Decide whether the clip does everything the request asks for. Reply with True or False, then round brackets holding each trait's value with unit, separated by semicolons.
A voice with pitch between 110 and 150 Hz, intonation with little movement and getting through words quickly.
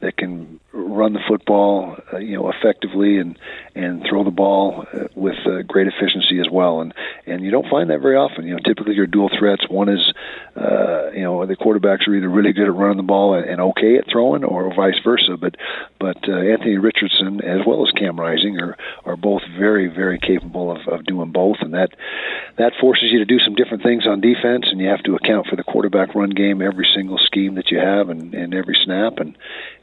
False (100 Hz; 2.0 semitones; 225 wpm)